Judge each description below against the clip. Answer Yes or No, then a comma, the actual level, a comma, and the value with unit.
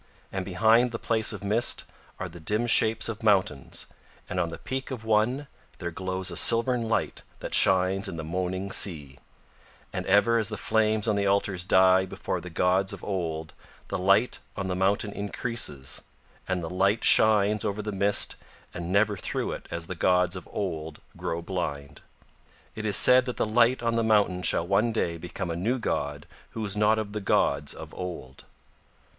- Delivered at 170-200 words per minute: Yes, average, 185 wpm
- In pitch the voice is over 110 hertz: No, low, 100 Hz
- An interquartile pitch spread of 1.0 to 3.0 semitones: No, average, 3.4 semitones